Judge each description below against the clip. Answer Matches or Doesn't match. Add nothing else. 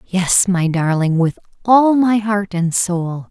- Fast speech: Doesn't match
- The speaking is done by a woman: Matches